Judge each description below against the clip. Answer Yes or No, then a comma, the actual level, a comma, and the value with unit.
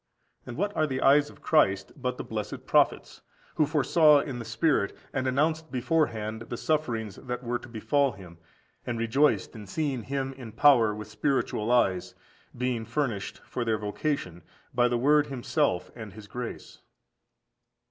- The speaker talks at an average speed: Yes, average, 160 wpm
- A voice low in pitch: Yes, low, 125 Hz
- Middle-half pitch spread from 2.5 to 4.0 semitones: No, average, 4.6 semitones